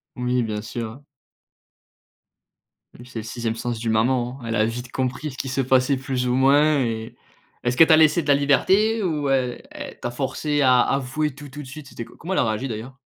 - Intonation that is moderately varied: Yes, average, 3.1 semitones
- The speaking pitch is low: Yes, low, 130 Hz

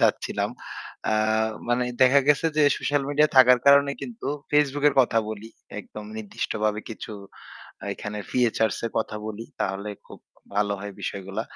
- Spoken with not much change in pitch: No, average, 4.9 semitones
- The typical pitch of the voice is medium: No, low, 115 Hz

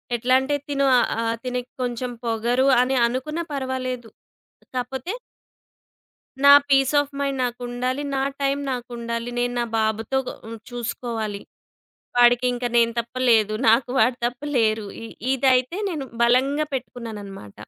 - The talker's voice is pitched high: Yes, high, 245 Hz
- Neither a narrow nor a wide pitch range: No, narrow, 2.2 semitones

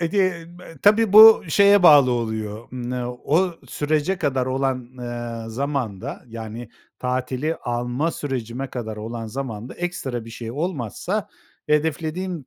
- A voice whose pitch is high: No, low, 130 Hz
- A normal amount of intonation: No, wide, 5.9 semitones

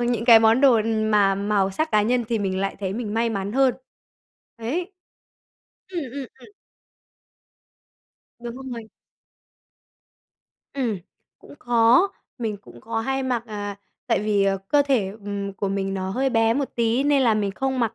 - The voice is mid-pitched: No, high, 225 Hz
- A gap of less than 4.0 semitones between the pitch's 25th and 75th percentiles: Yes, average, 3.6 semitones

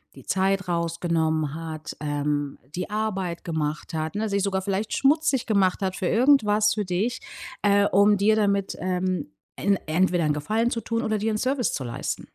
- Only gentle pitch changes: No, average, 4.2 semitones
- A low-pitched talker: No, high, 195 Hz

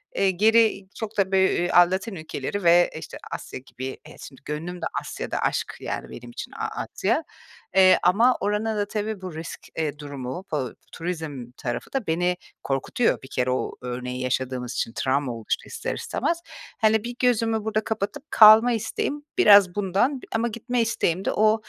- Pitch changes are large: Yes, wide, 7.4 semitones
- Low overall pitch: No, high, 190 Hz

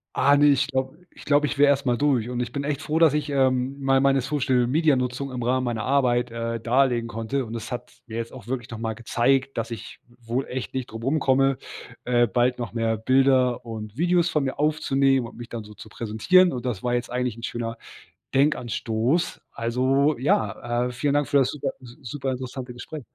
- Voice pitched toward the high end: No, low, 125 Hz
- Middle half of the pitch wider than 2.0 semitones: Yes, average, 2.7 semitones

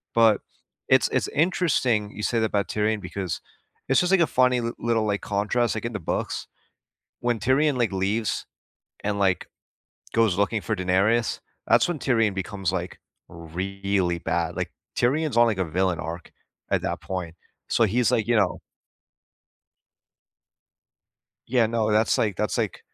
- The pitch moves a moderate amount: Yes, average, 3.7 semitones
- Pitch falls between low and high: No, low, 105 Hz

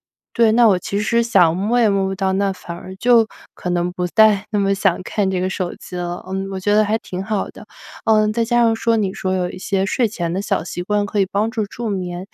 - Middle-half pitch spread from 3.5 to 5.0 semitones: No, average, 2.7 semitones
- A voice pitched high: Yes, high, 195 Hz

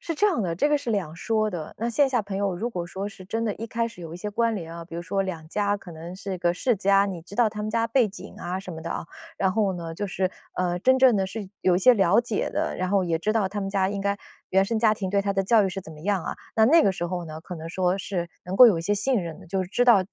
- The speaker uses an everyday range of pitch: Yes, average, 3.6 semitones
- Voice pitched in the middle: No, high, 195 Hz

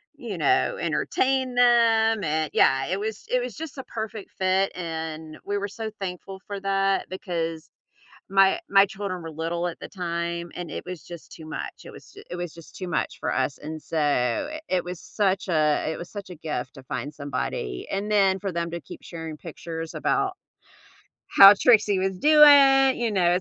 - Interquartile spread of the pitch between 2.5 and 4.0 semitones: No, average, 4.4 semitones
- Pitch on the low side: No, medium, 185 Hz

